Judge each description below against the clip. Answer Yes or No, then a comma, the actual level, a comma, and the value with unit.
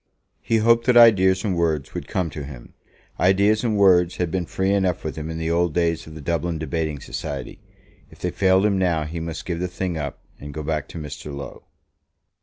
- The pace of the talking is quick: Yes, fast, 215 wpm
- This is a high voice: No, very low, 85 Hz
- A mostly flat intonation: No, average, 3.2 semitones